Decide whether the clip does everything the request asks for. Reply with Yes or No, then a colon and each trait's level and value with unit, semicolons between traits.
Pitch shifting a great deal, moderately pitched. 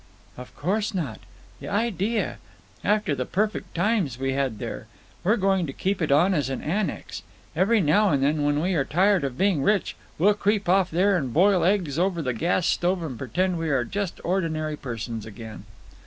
Yes: wide, 5.9 semitones; medium, 175 Hz